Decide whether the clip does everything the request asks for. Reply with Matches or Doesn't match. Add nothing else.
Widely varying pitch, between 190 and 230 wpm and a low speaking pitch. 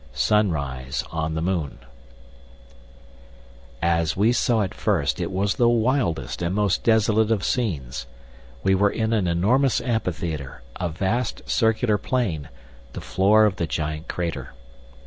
Doesn't match